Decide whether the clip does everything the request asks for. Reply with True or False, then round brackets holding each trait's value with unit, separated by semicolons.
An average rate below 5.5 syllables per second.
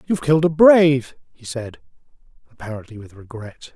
False (5.8 syllables/s)